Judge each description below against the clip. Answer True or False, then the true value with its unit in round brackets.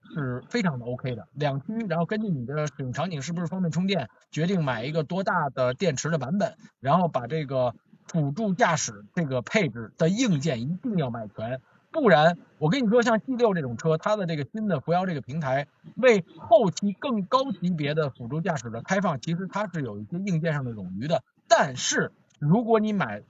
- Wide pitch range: True (6.6 semitones)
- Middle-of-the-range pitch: True (165 Hz)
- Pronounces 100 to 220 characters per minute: False (305 characters per minute)